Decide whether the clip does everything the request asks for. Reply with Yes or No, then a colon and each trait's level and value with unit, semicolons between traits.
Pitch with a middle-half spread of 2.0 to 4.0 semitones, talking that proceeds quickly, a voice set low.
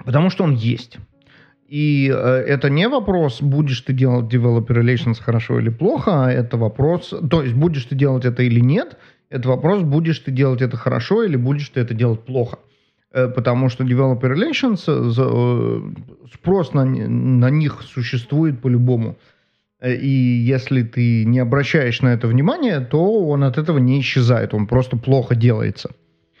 Yes: average, 3.0 semitones; fast, 165 wpm; low, 130 Hz